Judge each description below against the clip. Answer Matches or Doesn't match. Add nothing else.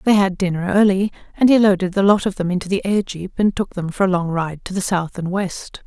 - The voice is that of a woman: Matches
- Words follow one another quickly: Matches